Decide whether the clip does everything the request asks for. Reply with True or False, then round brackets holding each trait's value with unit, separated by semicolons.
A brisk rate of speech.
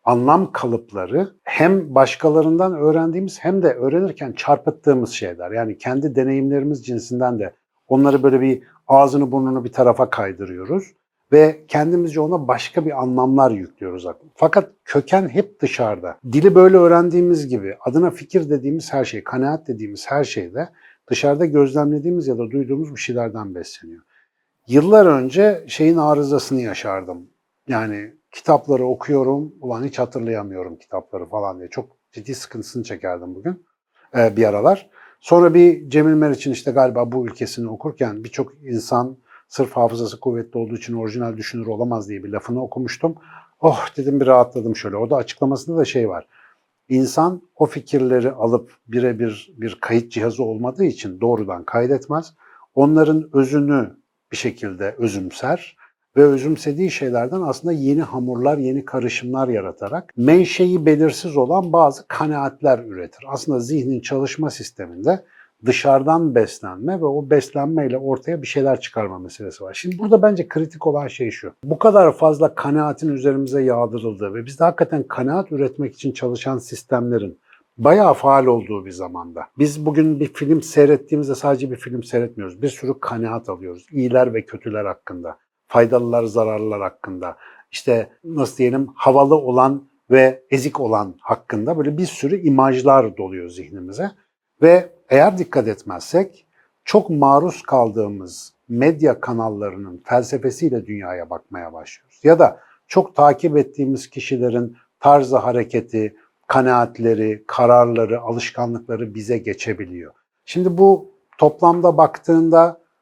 False (130 wpm)